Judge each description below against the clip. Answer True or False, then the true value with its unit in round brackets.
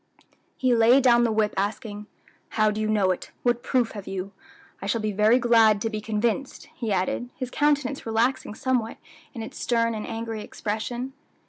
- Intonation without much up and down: True (2.3 semitones)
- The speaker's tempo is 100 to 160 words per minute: False (185 wpm)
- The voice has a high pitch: True (225 Hz)